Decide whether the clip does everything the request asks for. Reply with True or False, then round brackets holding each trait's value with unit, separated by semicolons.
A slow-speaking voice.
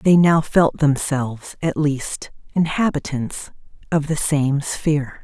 True (125 wpm)